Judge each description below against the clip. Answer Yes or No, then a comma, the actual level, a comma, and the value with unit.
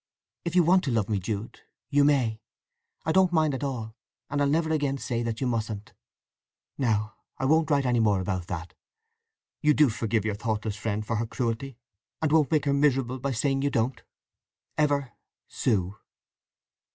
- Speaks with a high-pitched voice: No, low, 125 Hz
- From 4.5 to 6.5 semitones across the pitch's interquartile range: Yes, average, 4.8 semitones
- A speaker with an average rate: Yes, average, 175 wpm